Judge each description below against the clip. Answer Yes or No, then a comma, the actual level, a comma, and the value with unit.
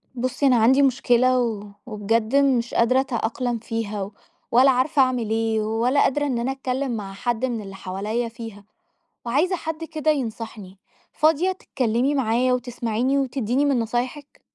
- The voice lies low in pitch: No, high, 245 Hz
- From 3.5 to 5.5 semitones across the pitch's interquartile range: No, average, 3.1 semitones